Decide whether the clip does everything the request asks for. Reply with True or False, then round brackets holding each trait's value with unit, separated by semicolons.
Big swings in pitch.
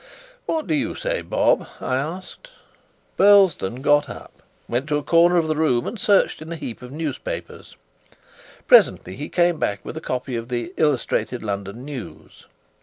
True (5.8 semitones)